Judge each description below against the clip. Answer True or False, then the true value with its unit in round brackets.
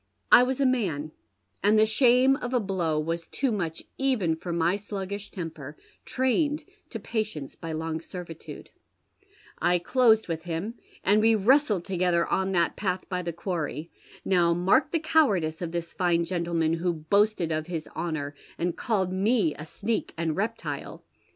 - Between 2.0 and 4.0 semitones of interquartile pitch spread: False (4.8 semitones)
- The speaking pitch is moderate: True (180 Hz)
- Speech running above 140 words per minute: True (165 wpm)